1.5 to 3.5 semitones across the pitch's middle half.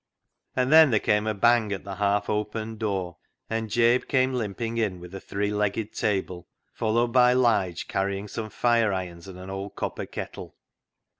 Yes: average, 3.1 semitones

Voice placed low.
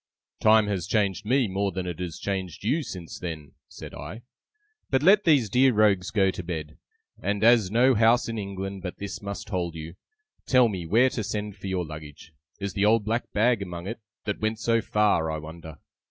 Yes: low, 100 Hz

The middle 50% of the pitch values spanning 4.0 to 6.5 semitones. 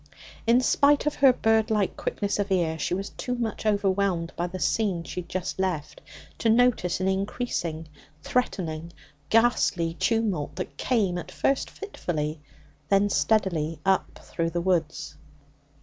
Yes: average, 4.7 semitones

